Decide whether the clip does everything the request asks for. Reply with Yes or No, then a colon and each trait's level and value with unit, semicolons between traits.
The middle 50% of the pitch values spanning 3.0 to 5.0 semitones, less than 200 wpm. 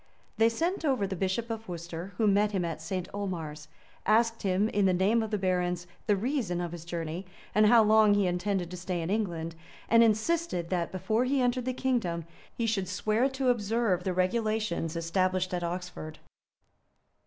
Yes: average, 4.1 semitones; average, 190 wpm